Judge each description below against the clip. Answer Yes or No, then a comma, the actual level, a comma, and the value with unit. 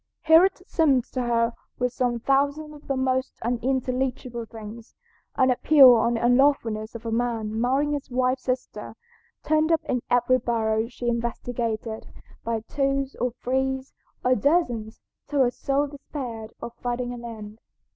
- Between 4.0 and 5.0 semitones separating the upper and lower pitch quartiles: No, average, 2.7 semitones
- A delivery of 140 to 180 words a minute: Yes, average, 155 wpm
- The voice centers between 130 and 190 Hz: No, very high, 250 Hz